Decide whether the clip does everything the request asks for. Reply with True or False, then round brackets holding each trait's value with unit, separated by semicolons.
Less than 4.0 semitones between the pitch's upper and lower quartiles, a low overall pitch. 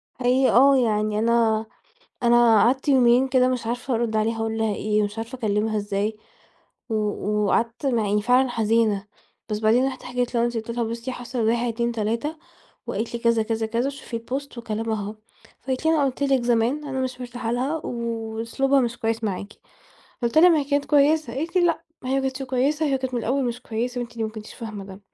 False (2.8 semitones; 235 Hz)